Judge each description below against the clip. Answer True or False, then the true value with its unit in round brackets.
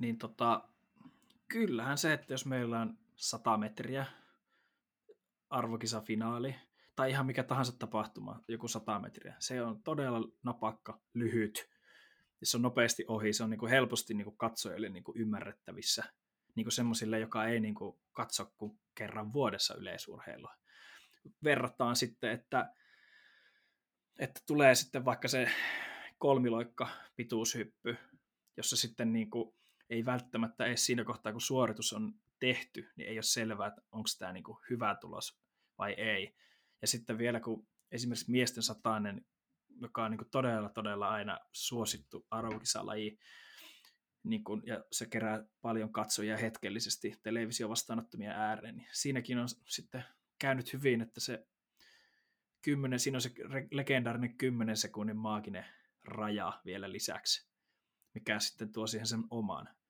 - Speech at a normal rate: True (130 wpm)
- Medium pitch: False (115 Hz)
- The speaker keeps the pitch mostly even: False (3.2 semitones)